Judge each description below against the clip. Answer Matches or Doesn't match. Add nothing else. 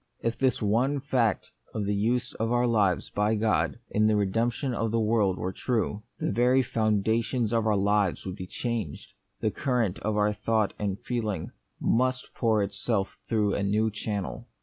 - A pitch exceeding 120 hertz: Doesn't match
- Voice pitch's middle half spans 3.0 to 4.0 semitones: Doesn't match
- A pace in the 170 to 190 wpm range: Matches